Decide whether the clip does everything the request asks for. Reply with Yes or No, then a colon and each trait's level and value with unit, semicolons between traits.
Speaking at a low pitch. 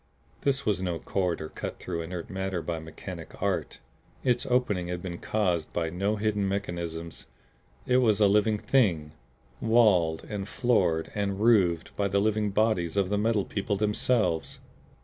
Yes: low, 100 Hz